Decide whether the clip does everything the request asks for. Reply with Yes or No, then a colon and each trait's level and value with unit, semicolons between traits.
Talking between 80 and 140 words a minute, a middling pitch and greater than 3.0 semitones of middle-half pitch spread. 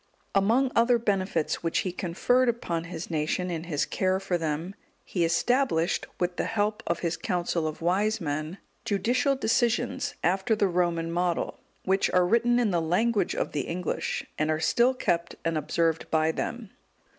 No: average, 170 wpm; medium, 180 Hz; average, 5.0 semitones